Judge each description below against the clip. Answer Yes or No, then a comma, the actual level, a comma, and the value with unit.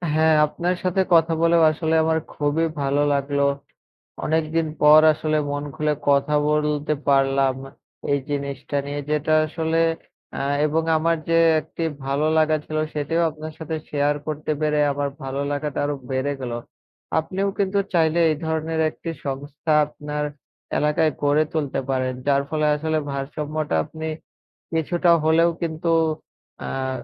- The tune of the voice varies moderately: No, narrow, 1.9 semitones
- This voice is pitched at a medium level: Yes, medium, 155 Hz